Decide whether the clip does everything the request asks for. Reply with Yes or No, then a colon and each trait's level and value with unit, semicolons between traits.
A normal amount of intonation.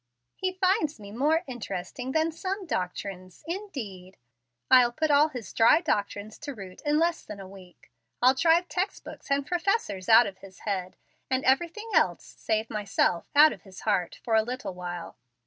No: wide, 8.3 semitones